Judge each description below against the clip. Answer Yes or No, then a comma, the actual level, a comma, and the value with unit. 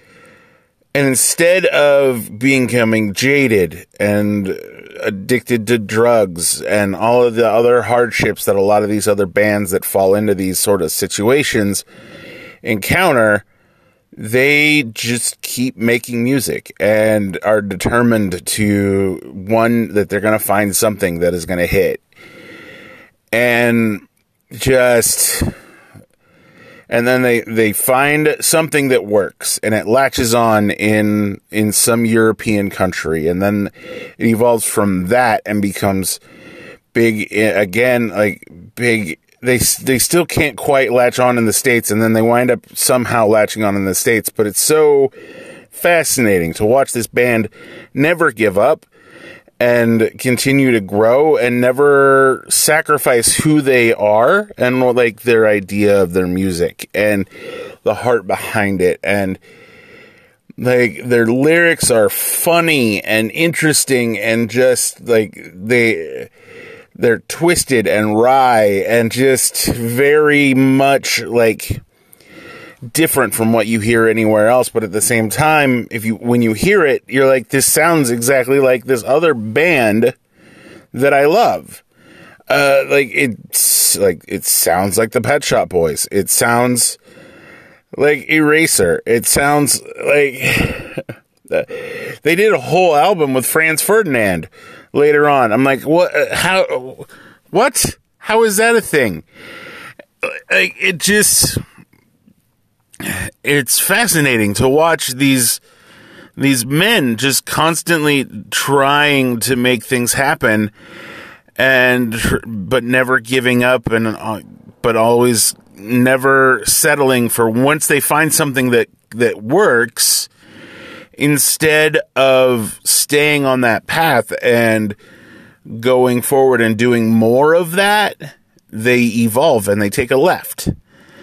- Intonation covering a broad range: No, average, 4.7 semitones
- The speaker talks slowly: Yes, slow, 130 wpm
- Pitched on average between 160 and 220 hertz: No, low, 120 Hz